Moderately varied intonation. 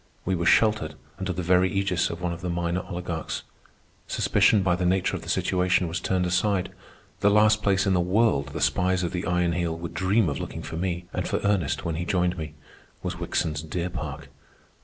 No: narrow, 1.8 semitones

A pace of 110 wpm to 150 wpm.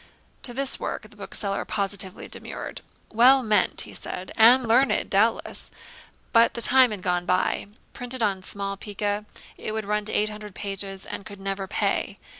No: average, 170 wpm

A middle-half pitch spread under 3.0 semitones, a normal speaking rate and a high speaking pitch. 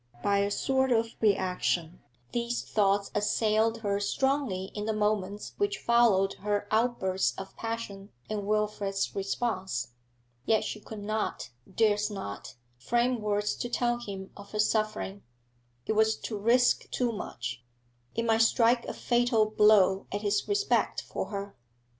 Yes: narrow, 2.5 semitones; average, 145 wpm; high, 210 Hz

